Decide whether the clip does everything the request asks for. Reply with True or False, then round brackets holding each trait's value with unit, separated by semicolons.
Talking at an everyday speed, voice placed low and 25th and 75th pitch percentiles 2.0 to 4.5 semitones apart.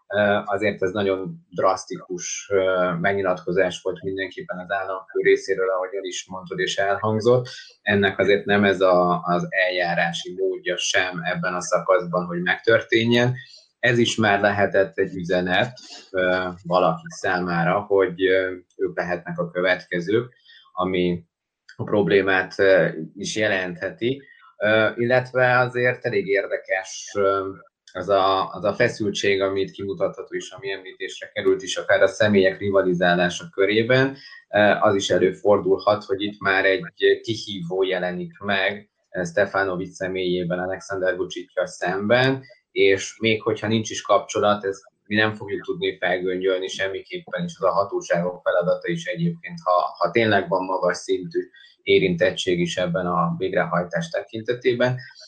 False (125 wpm; 100 Hz; 5.1 semitones)